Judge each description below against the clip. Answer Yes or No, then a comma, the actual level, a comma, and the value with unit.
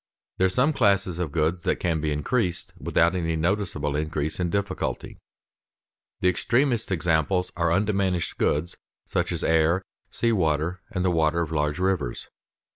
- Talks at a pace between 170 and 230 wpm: No, average, 150 wpm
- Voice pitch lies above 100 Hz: No, very low, 85 Hz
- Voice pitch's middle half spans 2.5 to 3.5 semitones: Yes, average, 3.1 semitones